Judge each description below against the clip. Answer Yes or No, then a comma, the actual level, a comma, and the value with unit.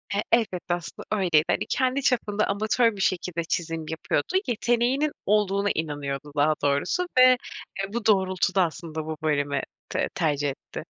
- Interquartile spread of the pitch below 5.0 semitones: No, wide, 5.6 semitones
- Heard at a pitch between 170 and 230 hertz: Yes, medium, 185 Hz